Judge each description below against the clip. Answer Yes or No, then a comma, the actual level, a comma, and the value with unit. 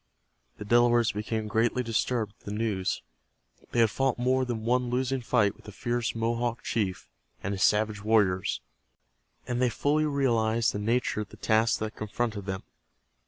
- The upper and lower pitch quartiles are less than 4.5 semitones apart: Yes, narrow, 2.4 semitones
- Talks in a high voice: No, low, 115 Hz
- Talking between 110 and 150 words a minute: No, average, 165 wpm